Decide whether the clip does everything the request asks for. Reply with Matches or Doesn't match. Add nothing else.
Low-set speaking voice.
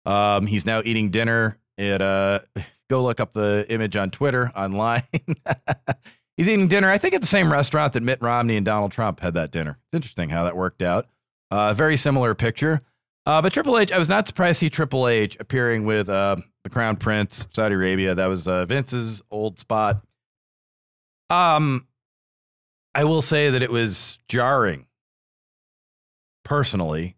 Matches